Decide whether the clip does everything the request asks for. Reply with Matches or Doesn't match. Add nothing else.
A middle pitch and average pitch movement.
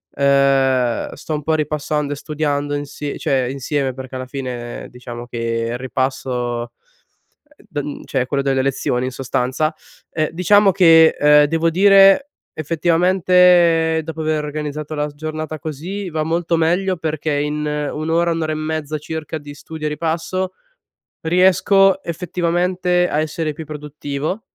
Matches